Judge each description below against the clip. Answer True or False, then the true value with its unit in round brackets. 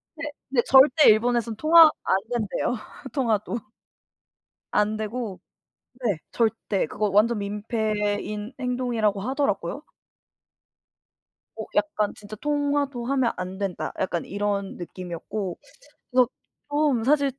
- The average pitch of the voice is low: False (220 Hz)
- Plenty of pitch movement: False (4.3 semitones)